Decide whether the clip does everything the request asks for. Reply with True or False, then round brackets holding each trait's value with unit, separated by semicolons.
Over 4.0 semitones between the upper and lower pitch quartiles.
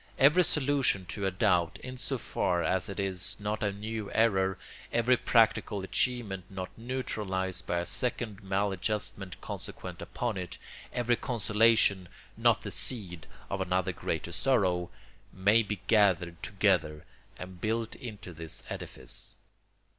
False (3.6 semitones)